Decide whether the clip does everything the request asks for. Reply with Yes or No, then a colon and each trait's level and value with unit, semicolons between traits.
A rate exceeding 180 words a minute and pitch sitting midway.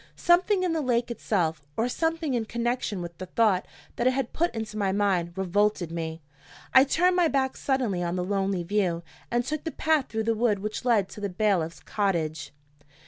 No: average, 195 wpm; high, 215 Hz